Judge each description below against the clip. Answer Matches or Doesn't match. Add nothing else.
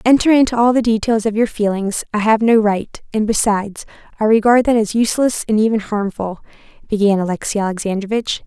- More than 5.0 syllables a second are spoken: Matches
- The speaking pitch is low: Doesn't match